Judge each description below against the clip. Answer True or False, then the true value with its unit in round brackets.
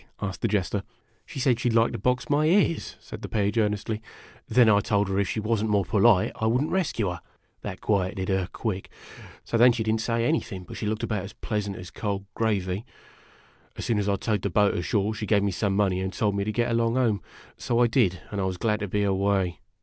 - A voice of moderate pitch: False (105 Hz)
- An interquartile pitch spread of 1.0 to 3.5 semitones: True (2.8 semitones)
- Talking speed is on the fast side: True (250 wpm)